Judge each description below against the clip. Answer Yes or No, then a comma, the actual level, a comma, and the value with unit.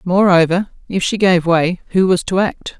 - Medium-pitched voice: Yes, medium, 180 Hz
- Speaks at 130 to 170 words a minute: No, average, 195 wpm